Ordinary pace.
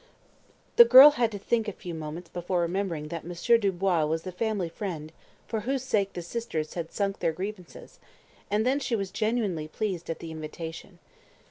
Yes: average, 180 wpm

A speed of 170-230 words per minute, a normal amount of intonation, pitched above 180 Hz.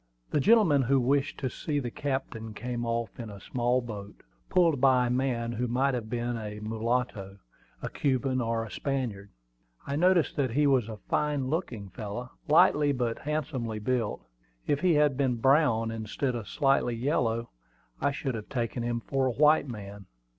No: average, 175 wpm; average, 3.5 semitones; low, 125 Hz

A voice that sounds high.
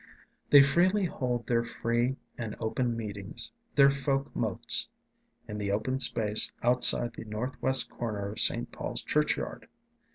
No: low, 120 Hz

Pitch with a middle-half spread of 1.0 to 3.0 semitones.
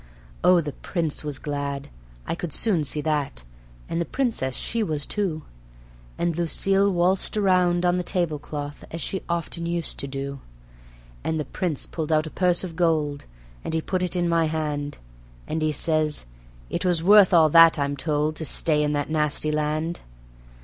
Yes: average, 2.7 semitones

